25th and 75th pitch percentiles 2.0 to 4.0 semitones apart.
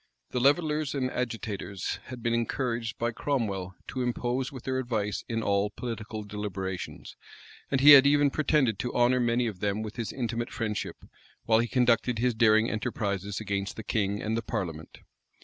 Yes: average, 3.2 semitones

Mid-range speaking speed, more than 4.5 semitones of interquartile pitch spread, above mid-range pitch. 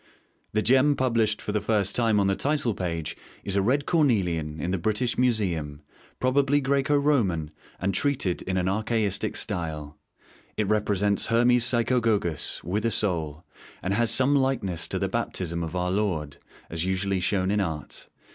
No: average, 165 wpm; average, 5.2 semitones; low, 100 Hz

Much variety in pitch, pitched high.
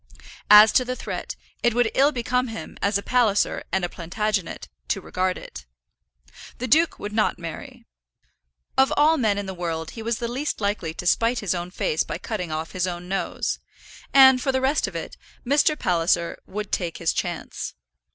Yes: wide, 5.9 semitones; high, 210 Hz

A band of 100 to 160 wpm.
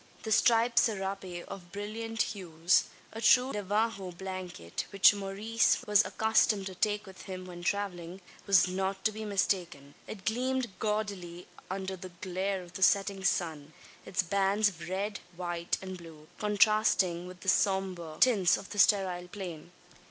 Yes: average, 150 wpm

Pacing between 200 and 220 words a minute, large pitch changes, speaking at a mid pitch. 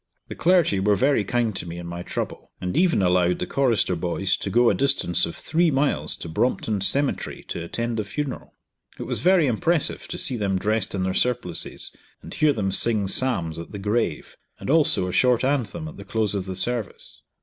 No: fast, 205 wpm; wide, 6.3 semitones; low, 110 Hz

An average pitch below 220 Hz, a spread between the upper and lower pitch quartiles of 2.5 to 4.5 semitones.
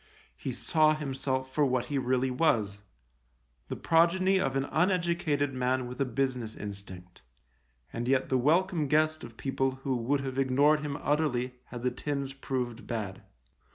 Yes: low, 135 Hz; average, 3.5 semitones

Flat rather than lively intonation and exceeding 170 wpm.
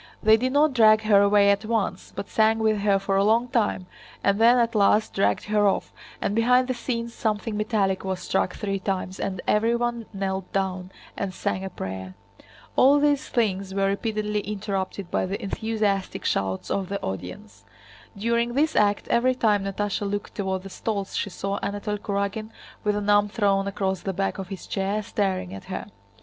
Yes: narrow, 2.3 semitones; average, 185 wpm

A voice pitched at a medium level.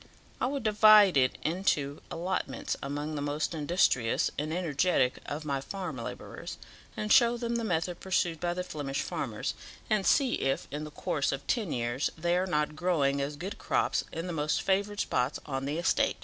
Yes: medium, 160 Hz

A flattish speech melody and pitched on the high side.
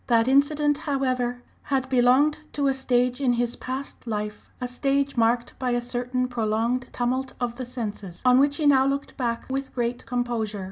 Yes: narrow, 2.1 semitones; very high, 250 Hz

